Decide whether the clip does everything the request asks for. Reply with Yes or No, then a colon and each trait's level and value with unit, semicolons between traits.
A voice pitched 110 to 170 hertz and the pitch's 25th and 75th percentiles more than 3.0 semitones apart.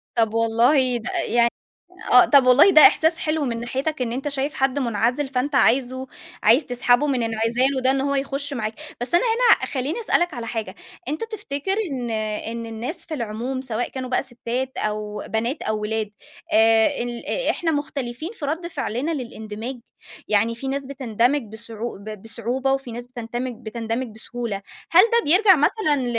No: very high, 250 Hz; average, 3.7 semitones